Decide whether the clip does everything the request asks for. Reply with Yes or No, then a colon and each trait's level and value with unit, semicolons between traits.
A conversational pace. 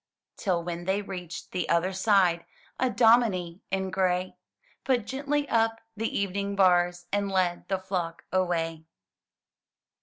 No: slow, 130 wpm